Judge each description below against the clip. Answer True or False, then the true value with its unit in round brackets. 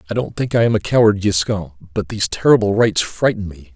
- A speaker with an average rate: False (225 wpm)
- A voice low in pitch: True (100 Hz)